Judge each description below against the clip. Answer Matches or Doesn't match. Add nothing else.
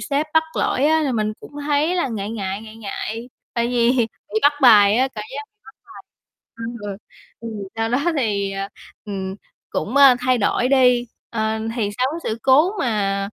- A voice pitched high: Matches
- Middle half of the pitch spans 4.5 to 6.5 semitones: Doesn't match